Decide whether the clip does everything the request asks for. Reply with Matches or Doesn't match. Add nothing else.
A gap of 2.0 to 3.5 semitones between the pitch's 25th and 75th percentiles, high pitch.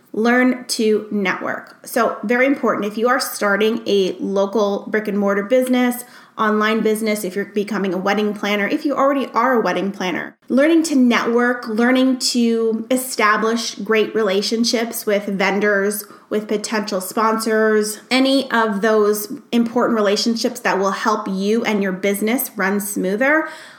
Matches